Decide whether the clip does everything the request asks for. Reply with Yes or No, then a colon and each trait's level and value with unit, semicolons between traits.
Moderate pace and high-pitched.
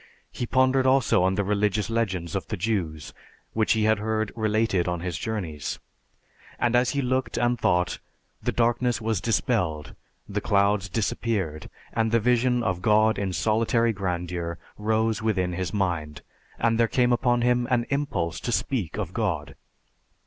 No: average, 160 wpm; low, 110 Hz